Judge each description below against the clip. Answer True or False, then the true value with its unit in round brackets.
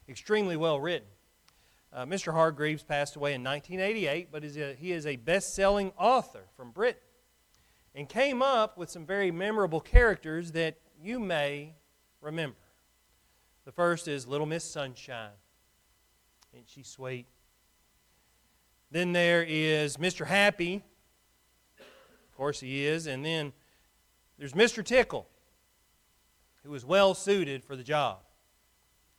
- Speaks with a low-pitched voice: False (155 Hz)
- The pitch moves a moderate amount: True (4.7 semitones)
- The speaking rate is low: True (130 wpm)